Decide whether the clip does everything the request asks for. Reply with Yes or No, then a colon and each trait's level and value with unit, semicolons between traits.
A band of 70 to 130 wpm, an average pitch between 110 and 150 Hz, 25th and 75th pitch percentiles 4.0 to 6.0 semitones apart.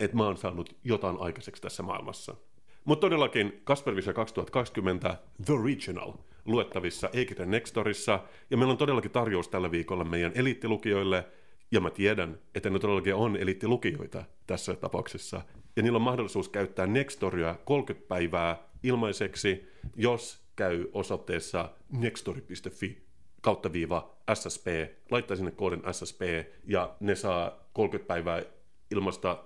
No: average, 120 wpm; very low, 95 Hz; average, 4.5 semitones